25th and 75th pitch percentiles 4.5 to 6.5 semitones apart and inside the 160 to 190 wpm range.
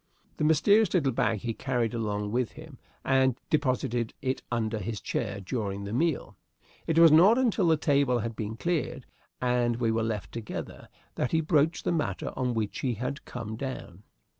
Yes: wide, 5.4 semitones; average, 180 wpm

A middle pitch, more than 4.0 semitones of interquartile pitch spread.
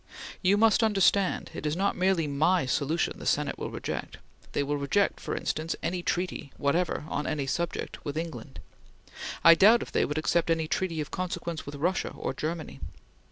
No: medium, 165 Hz; average, 3.7 semitones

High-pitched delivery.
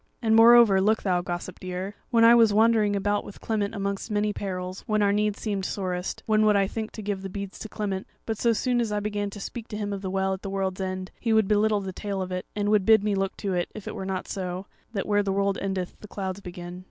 Yes: high, 200 Hz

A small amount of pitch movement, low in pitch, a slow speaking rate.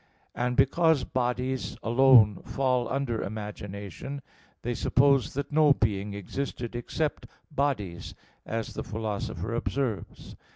No: average, 4.2 semitones; low, 125 Hz; slow, 115 wpm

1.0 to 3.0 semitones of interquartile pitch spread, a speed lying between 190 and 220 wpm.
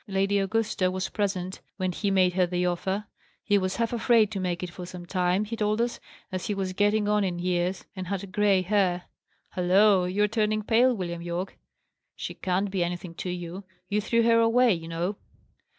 Yes: average, 2.7 semitones; average, 200 wpm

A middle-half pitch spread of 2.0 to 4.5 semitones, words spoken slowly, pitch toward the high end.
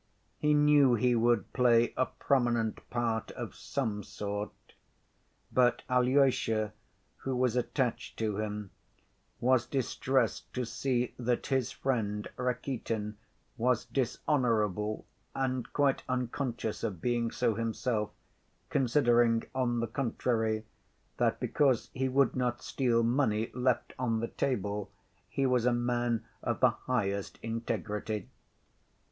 No: narrow, 2.4 semitones; slow, 120 wpm; low, 120 Hz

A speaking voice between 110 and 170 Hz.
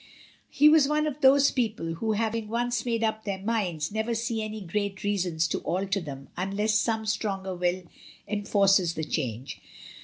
No: high, 210 Hz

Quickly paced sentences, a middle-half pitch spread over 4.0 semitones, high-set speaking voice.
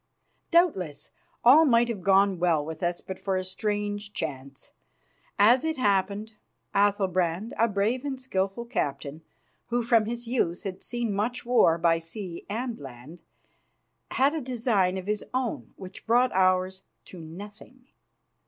No: average, 145 wpm; average, 4.6 semitones; high, 205 Hz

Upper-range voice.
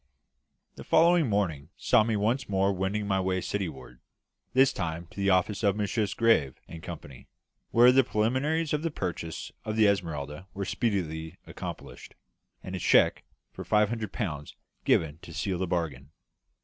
No: low, 100 Hz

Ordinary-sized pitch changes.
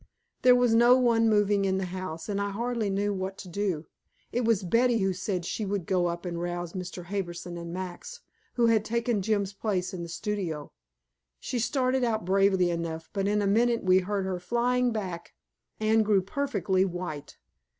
Yes: average, 3.8 semitones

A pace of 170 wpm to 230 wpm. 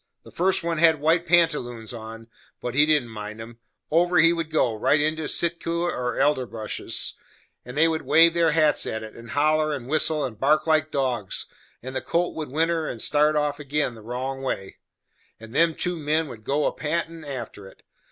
Yes: average, 200 wpm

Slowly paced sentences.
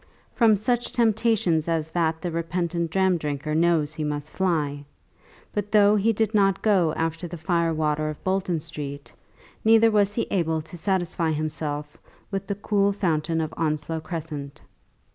No: average, 160 wpm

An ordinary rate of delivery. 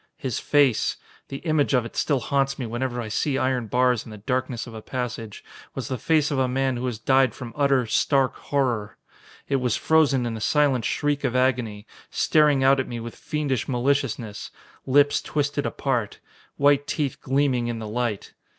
Yes: average, 185 wpm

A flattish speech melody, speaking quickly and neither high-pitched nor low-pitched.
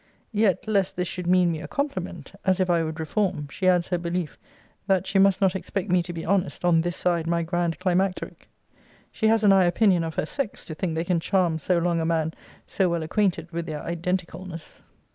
Yes: narrow, 2.2 semitones; fast, 220 wpm; medium, 175 Hz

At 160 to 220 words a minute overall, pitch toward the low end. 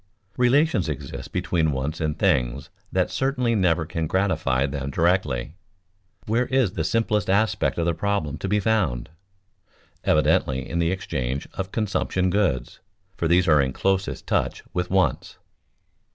No: average, 145 wpm; very low, 90 Hz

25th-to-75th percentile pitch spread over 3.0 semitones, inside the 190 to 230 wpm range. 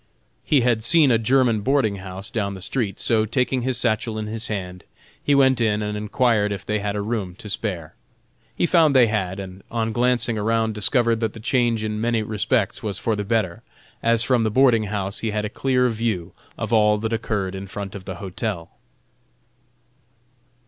No: average, 2.7 semitones; average, 195 wpm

